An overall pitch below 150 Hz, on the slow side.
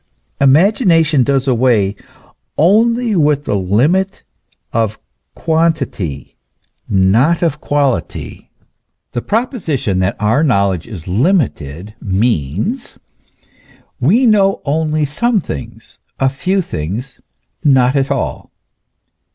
Yes: low, 135 Hz; slow, 95 wpm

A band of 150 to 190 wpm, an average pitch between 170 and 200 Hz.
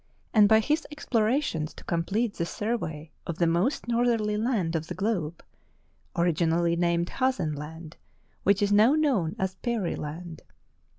Yes: average, 160 wpm; high, 190 Hz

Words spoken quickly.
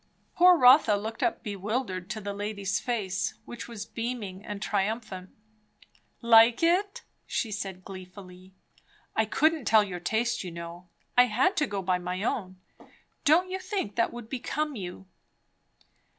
No: average, 150 wpm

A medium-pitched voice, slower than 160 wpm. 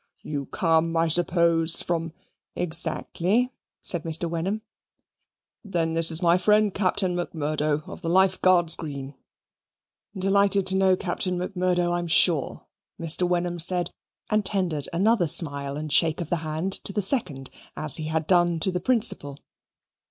Yes: medium, 175 Hz; average, 150 wpm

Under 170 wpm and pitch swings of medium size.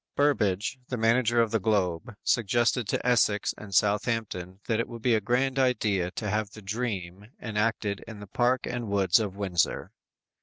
No: average, 175 wpm; average, 3.0 semitones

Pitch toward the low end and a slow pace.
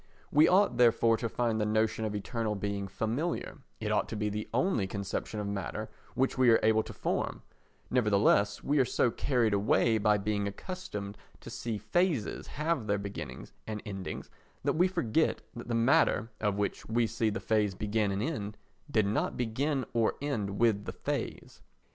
No: low, 110 Hz; average, 180 wpm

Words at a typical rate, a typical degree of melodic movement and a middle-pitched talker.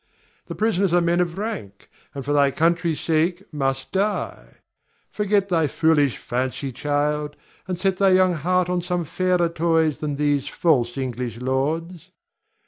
Yes: average, 150 wpm; average, 4.1 semitones; medium, 160 Hz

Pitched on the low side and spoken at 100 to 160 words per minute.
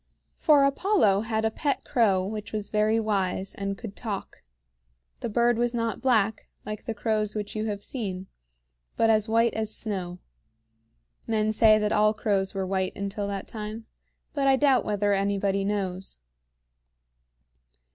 No: high, 215 Hz; average, 155 wpm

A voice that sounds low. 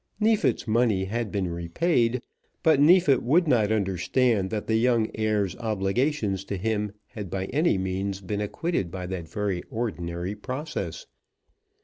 Yes: low, 105 Hz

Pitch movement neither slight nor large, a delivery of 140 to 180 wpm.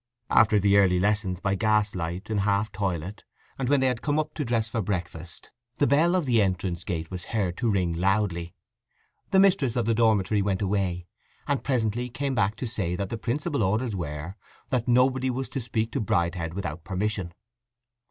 No: average, 4.7 semitones; average, 190 wpm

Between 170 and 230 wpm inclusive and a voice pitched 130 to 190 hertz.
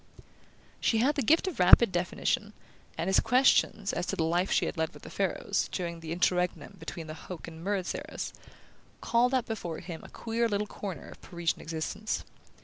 Yes: average, 190 wpm; medium, 185 Hz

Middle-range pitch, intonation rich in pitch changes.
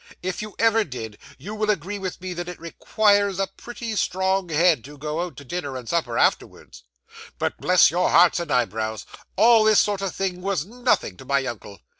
Yes: medium, 180 Hz; wide, 5.8 semitones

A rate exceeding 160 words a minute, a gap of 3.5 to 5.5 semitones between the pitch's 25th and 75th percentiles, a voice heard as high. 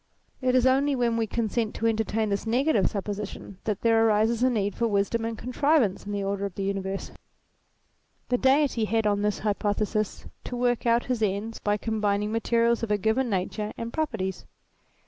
No: average, 185 wpm; narrow, 2.5 semitones; high, 220 Hz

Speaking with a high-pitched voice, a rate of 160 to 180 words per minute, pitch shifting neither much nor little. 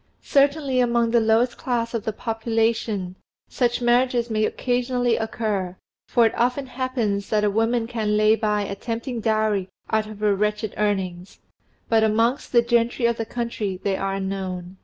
No: high, 225 Hz; average, 165 wpm; narrow, 2.3 semitones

